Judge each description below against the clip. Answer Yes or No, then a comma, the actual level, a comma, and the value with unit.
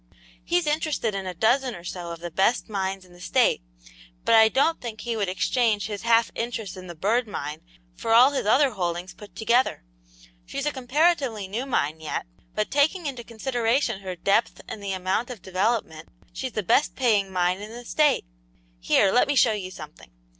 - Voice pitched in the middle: No, high, 220 Hz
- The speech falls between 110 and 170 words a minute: No, average, 195 wpm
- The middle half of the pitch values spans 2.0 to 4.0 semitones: No, average, 5.0 semitones